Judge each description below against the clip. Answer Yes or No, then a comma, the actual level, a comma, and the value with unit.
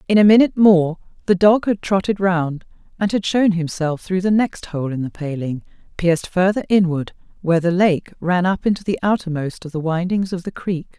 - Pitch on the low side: No, medium, 180 Hz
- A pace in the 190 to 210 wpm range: Yes, average, 200 wpm